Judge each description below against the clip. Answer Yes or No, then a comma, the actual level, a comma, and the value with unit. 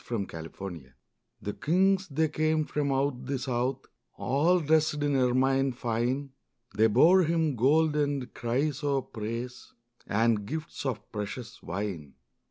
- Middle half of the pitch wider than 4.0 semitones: Yes, average, 4.5 semitones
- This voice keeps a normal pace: No, slow, 125 wpm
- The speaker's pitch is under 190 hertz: Yes, low, 135 Hz